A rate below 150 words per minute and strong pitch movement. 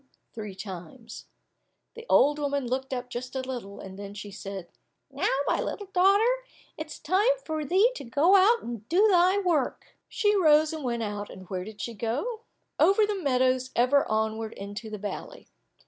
No: average, 180 wpm; wide, 9.0 semitones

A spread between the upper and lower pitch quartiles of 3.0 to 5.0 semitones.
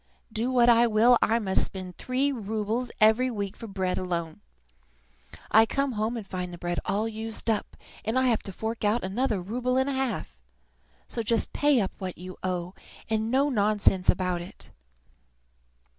Yes: average, 4.2 semitones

